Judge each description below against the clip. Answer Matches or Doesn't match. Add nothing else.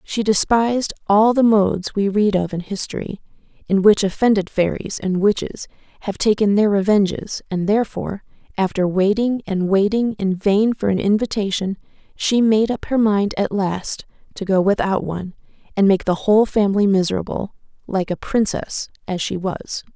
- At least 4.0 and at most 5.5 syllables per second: Matches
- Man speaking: Doesn't match